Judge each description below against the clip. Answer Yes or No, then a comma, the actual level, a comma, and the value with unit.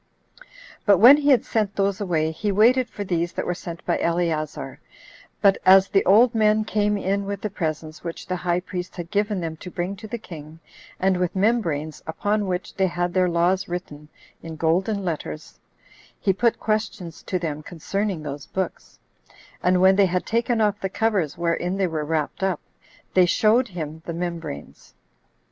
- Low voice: No, medium, 185 Hz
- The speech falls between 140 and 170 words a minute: No, average, 185 wpm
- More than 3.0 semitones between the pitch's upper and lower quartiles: Yes, average, 3.4 semitones